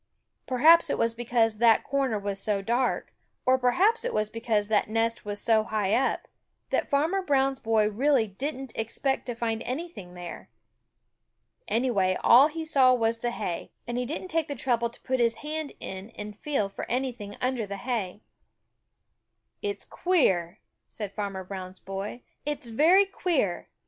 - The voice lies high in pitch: Yes, high, 235 Hz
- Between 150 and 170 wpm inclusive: Yes, average, 165 wpm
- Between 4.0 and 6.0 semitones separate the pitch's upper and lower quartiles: Yes, average, 4.6 semitones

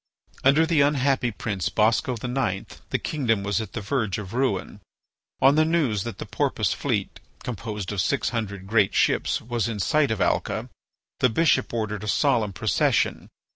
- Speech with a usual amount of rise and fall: Yes, average, 4.5 semitones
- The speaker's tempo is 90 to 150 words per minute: No, average, 170 wpm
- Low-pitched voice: Yes, low, 115 Hz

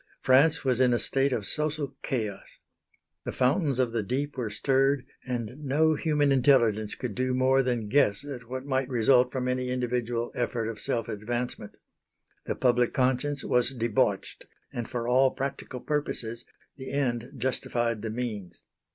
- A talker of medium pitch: No, low, 125 Hz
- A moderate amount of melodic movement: No, narrow, 2.3 semitones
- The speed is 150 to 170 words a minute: Yes, average, 160 wpm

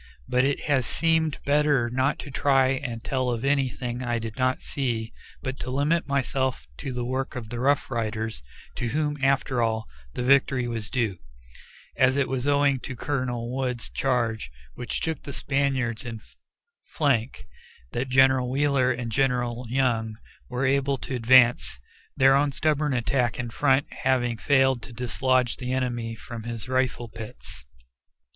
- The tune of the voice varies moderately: No, narrow, 2.3 semitones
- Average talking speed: Yes, average, 160 wpm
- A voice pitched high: No, low, 130 Hz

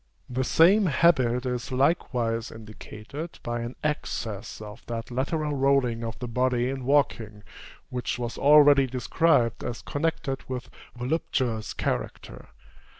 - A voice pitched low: Yes, low, 125 Hz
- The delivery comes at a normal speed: No, slow, 125 wpm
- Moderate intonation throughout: Yes, average, 3.4 semitones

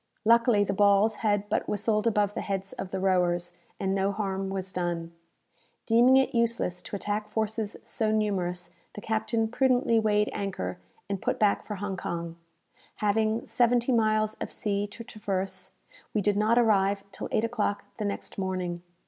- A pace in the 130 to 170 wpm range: Yes, average, 165 wpm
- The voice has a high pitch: Yes, high, 205 Hz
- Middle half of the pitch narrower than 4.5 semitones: Yes, narrow, 2.4 semitones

